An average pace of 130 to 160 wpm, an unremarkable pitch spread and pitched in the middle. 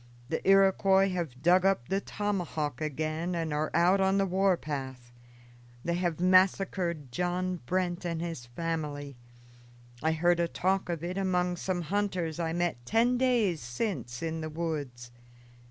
Yes: average, 155 wpm; average, 3.2 semitones; medium, 175 Hz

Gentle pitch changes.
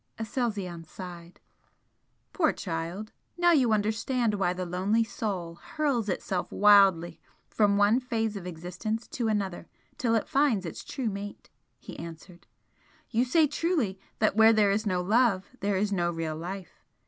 No: average, 4.0 semitones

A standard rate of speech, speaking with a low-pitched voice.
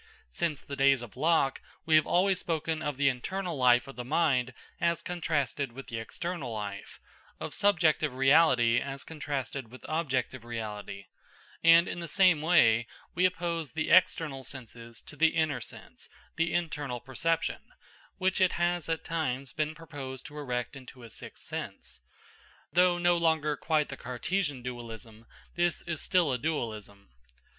No: average, 155 wpm; medium, 145 Hz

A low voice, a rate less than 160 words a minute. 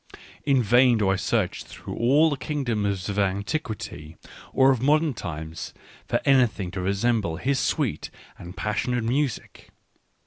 Yes: low, 115 Hz; average, 145 wpm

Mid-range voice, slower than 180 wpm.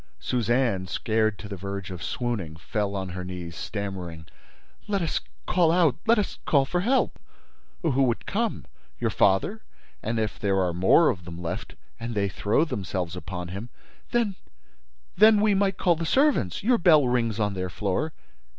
No: low, 110 Hz; average, 150 wpm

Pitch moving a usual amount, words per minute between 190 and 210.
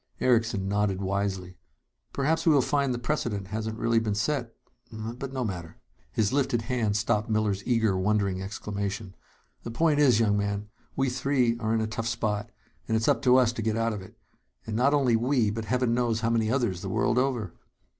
Yes: average, 3.3 semitones; average, 200 wpm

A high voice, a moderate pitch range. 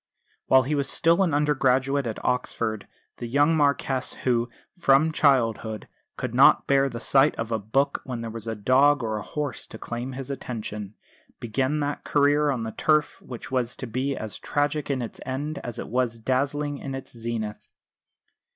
No: low, 130 Hz; average, 3.6 semitones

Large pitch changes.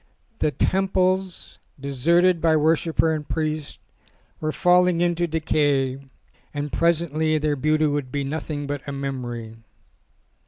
No: average, 3.0 semitones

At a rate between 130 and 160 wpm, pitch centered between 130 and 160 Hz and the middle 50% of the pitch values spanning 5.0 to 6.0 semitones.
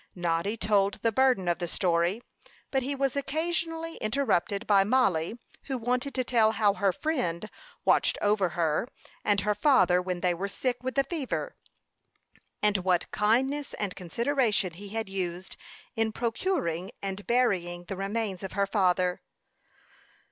No: average, 150 wpm; high, 205 Hz; wide, 5.6 semitones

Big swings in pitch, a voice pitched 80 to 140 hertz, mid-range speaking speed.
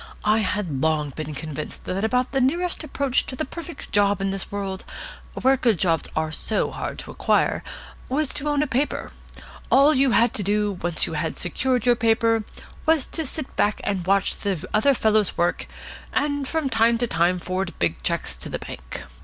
No: wide, 6.6 semitones; high, 215 Hz; average, 195 wpm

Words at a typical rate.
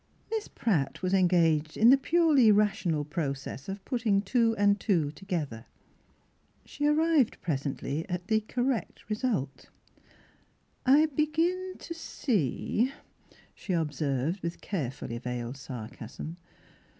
No: slow, 115 wpm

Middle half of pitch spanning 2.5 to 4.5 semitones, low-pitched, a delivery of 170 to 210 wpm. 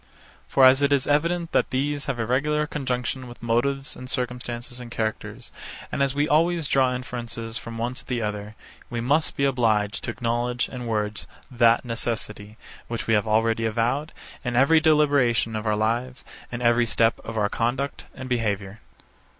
Yes: average, 3.2 semitones; low, 120 Hz; average, 180 wpm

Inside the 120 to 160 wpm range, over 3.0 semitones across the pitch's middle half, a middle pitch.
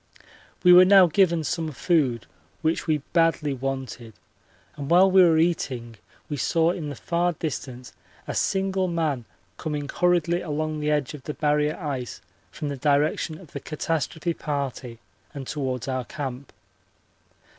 Yes: average, 150 wpm; average, 3.7 semitones; medium, 150 Hz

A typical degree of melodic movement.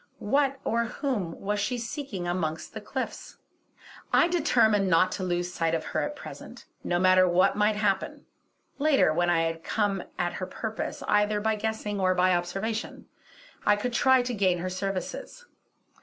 Yes: average, 4.0 semitones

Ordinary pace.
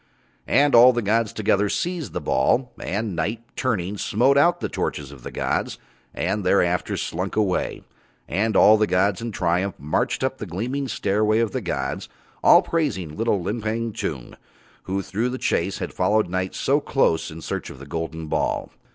Yes: average, 175 wpm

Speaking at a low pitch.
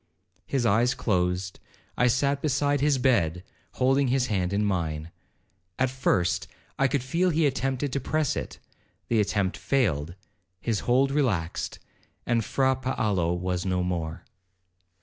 Yes: low, 120 Hz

